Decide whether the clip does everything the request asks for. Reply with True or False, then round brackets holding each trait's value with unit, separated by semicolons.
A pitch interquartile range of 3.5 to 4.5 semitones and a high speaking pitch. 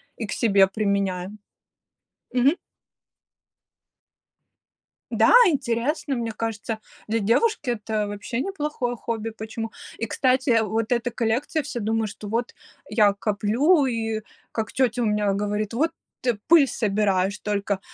False (3.0 semitones; 225 Hz)